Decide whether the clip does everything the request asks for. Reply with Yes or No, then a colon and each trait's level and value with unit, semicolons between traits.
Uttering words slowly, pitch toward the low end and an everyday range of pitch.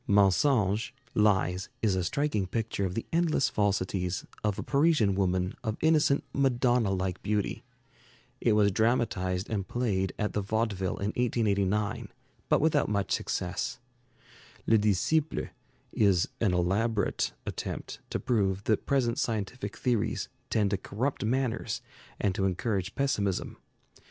Yes: slow, 130 wpm; low, 105 Hz; average, 3.8 semitones